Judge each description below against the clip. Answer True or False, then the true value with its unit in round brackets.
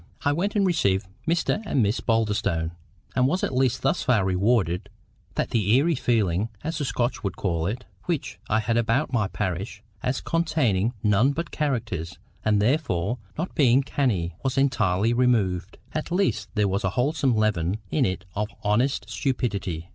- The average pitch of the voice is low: True (115 Hz)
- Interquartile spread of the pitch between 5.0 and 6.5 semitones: True (5.5 semitones)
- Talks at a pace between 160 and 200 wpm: True (165 wpm)